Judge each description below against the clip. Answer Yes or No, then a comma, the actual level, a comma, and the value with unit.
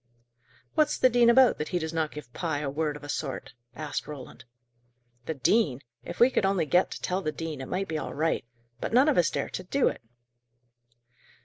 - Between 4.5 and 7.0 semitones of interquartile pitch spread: Yes, average, 4.8 semitones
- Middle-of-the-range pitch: Yes, medium, 160 Hz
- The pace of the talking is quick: Yes, fast, 210 wpm